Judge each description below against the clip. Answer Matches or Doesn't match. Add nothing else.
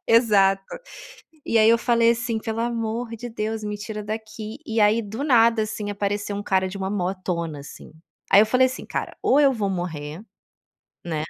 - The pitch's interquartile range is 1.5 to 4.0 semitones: Matches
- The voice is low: Doesn't match